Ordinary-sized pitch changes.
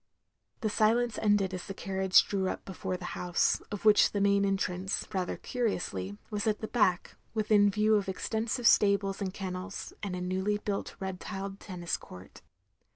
No: narrow, 2.2 semitones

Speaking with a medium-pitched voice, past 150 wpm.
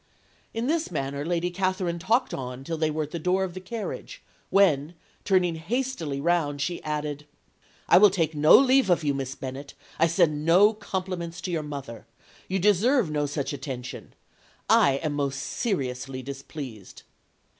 Yes: medium, 165 Hz; average, 160 wpm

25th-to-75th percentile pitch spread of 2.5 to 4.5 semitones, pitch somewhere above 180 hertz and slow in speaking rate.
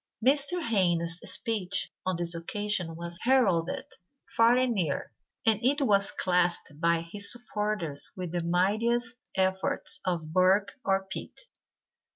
No: average, 4.9 semitones; high, 190 Hz; slow, 130 wpm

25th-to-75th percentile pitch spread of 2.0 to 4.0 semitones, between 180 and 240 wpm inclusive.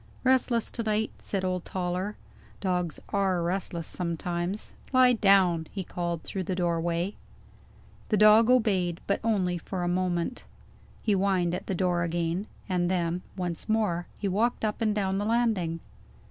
No: average, 3.3 semitones; average, 155 wpm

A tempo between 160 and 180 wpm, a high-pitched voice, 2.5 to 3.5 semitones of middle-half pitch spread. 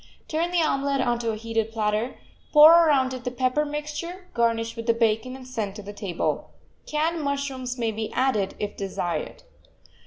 No: average, 175 wpm; very high, 250 Hz; average, 4.7 semitones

